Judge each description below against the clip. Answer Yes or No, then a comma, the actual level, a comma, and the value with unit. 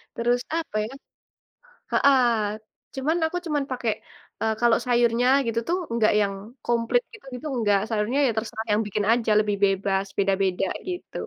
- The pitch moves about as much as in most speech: Yes, average, 3.5 semitones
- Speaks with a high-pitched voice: Yes, high, 230 Hz